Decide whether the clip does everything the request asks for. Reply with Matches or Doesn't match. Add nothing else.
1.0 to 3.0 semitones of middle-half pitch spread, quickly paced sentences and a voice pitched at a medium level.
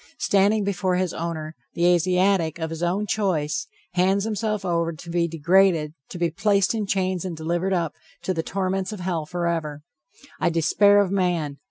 Doesn't match